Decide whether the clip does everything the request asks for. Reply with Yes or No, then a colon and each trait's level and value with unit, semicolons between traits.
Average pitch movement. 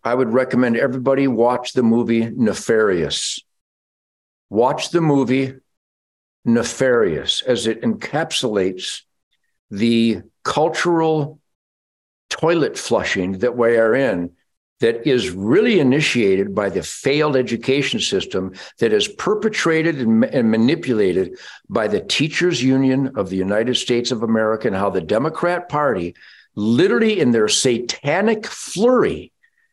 No: wide, 6.8 semitones